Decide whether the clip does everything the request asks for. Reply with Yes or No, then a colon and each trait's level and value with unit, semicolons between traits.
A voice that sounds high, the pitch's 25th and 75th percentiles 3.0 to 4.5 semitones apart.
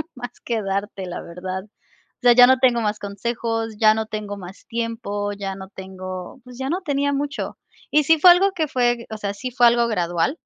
Yes: high, 225 Hz; average, 4.0 semitones